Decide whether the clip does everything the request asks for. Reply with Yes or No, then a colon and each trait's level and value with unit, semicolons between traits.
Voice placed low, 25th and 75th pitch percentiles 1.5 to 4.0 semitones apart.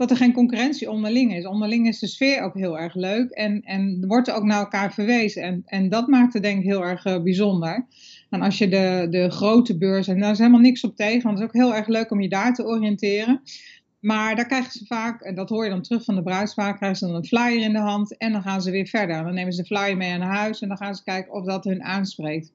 No: high, 205 Hz; average, 3.0 semitones